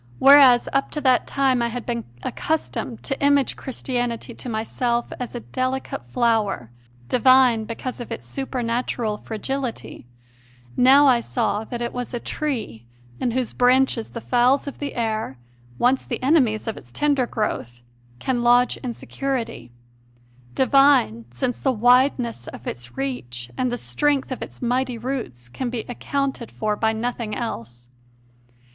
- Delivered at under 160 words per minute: Yes, average, 150 wpm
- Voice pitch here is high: Yes, high, 245 Hz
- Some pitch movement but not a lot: Yes, average, 3.0 semitones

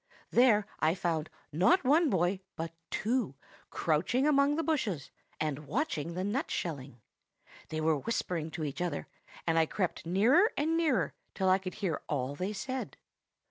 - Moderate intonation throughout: No, wide, 8.4 semitones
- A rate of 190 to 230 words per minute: No, average, 160 wpm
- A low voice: No, medium, 185 Hz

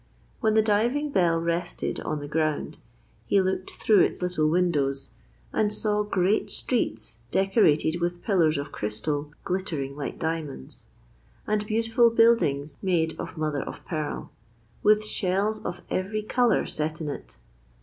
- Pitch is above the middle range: No, medium, 175 Hz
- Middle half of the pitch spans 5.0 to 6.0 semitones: Yes, wide, 5.5 semitones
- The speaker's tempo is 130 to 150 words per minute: Yes, average, 140 wpm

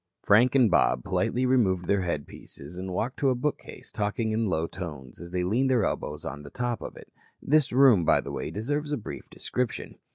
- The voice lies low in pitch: Yes, low, 110 Hz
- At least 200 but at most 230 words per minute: Yes, fast, 205 wpm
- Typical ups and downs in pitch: No, wide, 6.2 semitones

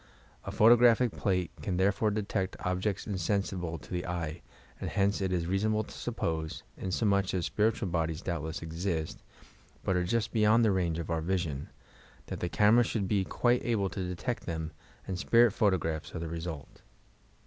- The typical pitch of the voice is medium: No, very low, 95 Hz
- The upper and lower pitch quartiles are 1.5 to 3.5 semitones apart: No, average, 4.0 semitones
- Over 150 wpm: Yes, average, 180 wpm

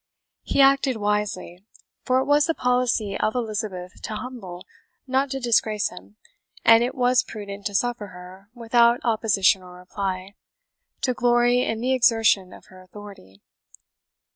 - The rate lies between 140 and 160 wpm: Yes, average, 145 wpm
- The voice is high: Yes, high, 220 Hz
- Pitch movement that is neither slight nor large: Yes, average, 4.1 semitones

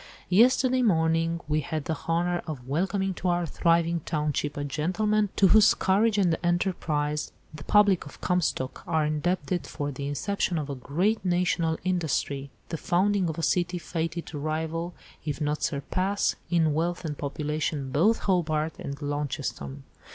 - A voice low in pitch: No, medium, 165 Hz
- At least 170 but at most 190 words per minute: No, average, 155 wpm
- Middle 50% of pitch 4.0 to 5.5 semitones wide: No, average, 3.4 semitones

